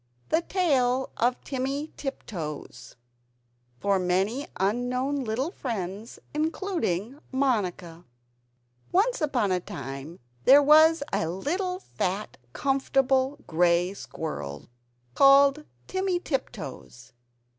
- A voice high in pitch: Yes, very high, 255 Hz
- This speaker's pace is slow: Yes, slow, 90 wpm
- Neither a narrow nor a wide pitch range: No, wide, 7.9 semitones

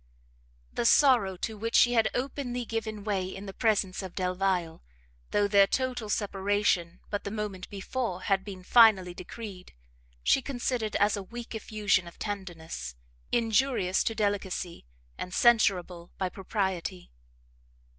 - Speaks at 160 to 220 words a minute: No, slow, 135 wpm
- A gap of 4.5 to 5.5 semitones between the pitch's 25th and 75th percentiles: No, average, 3.4 semitones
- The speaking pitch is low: No, high, 205 Hz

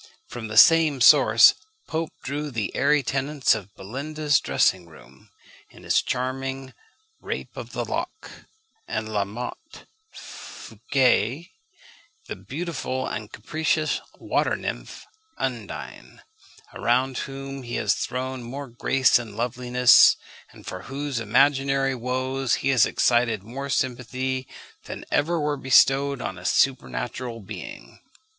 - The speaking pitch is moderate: No, low, 130 Hz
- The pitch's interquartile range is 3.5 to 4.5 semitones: No, average, 2.9 semitones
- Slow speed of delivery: Yes, slow, 125 wpm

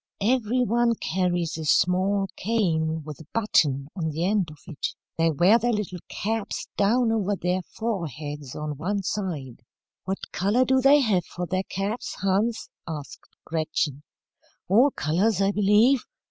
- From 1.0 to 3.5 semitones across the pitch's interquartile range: No, wide, 5.4 semitones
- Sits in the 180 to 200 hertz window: Yes, high, 190 Hz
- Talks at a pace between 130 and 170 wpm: Yes, average, 150 wpm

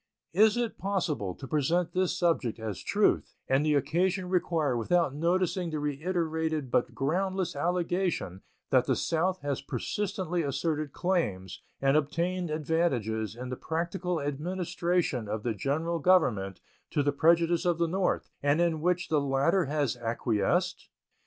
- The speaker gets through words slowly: No, average, 145 wpm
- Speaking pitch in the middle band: Yes, medium, 160 Hz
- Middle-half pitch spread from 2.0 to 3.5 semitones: No, average, 4.5 semitones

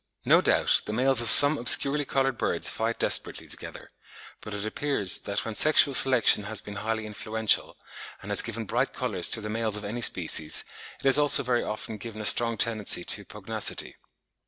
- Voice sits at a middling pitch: No, low, 115 Hz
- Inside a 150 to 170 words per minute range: No, average, 185 wpm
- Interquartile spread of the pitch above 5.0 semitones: No, average, 3.2 semitones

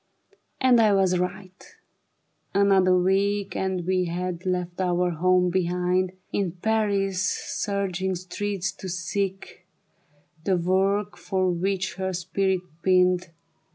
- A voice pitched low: No, medium, 185 Hz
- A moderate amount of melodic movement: No, narrow, 1.5 semitones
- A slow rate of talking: Yes, slow, 115 wpm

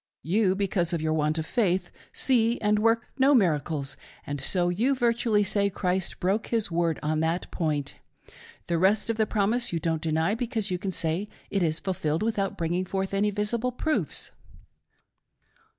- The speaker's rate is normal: Yes, average, 175 wpm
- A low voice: No, high, 190 Hz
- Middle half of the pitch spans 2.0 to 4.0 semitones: No, average, 4.8 semitones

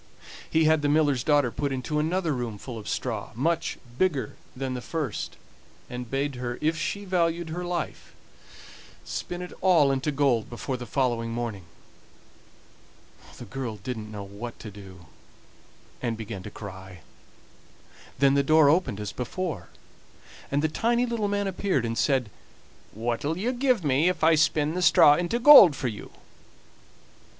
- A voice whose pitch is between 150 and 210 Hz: No, medium, 140 Hz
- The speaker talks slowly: No, average, 160 wpm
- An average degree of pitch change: No, wide, 6.0 semitones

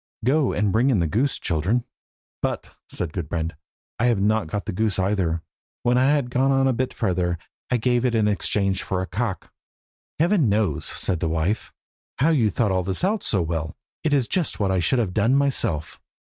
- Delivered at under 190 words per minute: No, average, 200 wpm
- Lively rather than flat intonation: Yes, wide, 5.7 semitones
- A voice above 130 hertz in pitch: No, low, 105 Hz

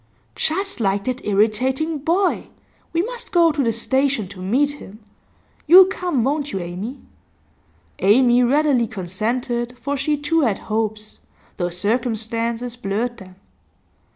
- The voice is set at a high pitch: Yes, high, 245 Hz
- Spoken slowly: Yes, slow, 130 wpm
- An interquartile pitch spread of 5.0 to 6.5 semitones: Yes, wide, 5.4 semitones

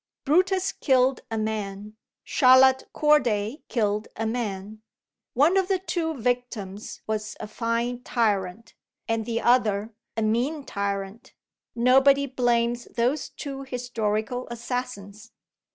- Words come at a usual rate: No, slow, 115 wpm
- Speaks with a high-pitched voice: Yes, high, 235 Hz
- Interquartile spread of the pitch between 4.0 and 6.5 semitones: No, average, 3.5 semitones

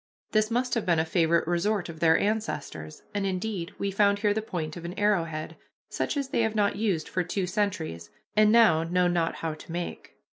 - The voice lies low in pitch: No, medium, 185 Hz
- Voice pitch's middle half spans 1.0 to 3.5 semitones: No, average, 4.3 semitones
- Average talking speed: No, fast, 215 wpm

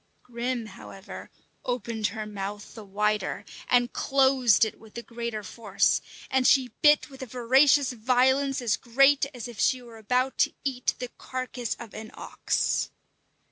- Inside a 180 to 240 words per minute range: No, average, 155 wpm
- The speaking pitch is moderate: No, high, 240 Hz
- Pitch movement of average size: Yes, average, 3.1 semitones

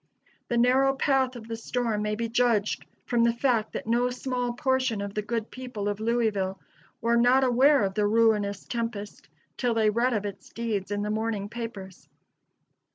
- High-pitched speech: Yes, high, 230 Hz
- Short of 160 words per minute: No, average, 180 wpm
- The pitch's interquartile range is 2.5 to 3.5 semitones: Yes, average, 2.8 semitones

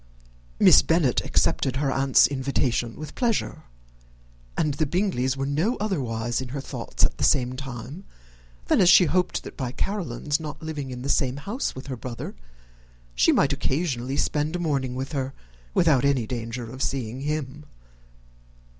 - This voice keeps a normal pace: Yes, average, 160 wpm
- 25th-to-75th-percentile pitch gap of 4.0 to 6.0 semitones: No, average, 3.3 semitones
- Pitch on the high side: No, low, 135 Hz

